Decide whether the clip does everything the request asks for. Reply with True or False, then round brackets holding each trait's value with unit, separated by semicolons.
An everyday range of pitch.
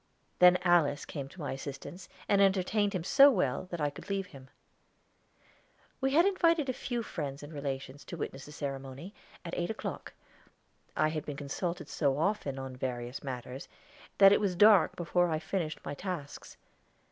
False (5.9 semitones)